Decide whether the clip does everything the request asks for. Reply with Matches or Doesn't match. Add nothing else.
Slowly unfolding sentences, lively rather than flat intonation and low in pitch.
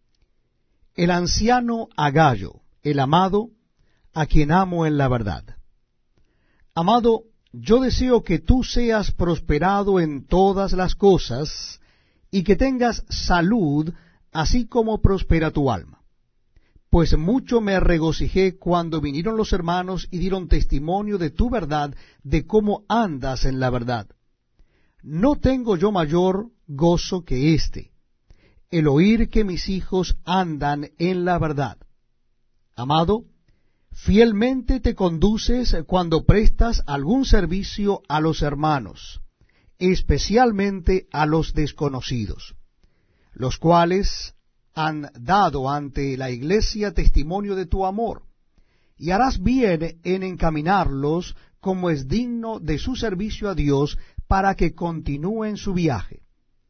Doesn't match